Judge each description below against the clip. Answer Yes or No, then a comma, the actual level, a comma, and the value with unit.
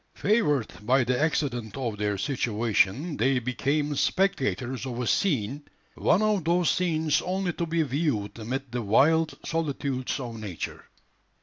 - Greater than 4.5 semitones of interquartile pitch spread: Yes, average, 5.3 semitones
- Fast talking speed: No, average, 140 wpm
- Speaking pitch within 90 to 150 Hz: Yes, low, 135 Hz